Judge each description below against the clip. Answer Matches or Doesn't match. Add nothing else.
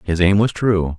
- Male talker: Matches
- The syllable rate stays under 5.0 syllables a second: Matches